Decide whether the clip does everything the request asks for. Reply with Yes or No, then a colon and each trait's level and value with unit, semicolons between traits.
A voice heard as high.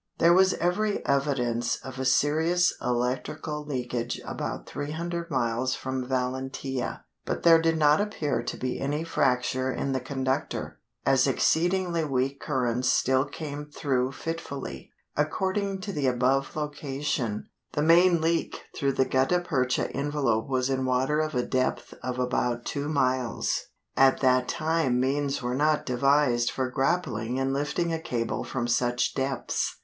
No: low, 135 Hz